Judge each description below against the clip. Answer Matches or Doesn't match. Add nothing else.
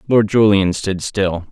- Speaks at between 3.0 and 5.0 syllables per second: Matches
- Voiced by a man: Matches